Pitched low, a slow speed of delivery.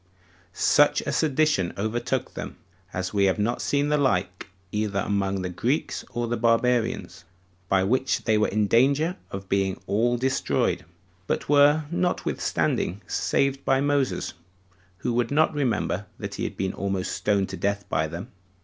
No: low, 115 Hz; average, 160 wpm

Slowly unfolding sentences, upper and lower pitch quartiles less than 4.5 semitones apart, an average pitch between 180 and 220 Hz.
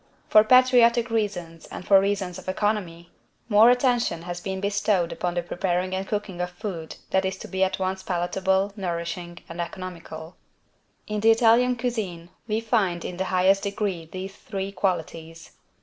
No: average, 165 wpm; average, 3.2 semitones; high, 190 Hz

